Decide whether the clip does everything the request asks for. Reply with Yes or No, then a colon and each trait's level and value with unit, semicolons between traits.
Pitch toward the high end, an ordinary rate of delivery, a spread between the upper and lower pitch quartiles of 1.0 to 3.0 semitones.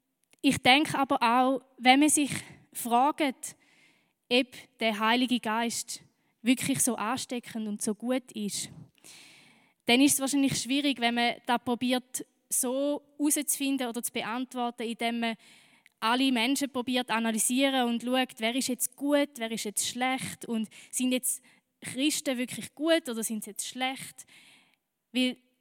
Yes: very high, 250 Hz; average, 145 wpm; narrow, 2.5 semitones